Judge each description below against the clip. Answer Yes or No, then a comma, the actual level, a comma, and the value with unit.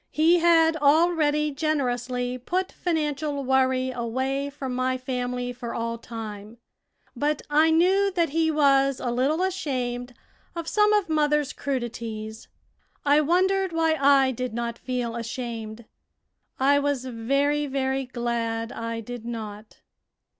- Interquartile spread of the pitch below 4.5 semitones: Yes, average, 4.1 semitones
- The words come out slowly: Yes, slow, 130 wpm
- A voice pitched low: No, very high, 265 Hz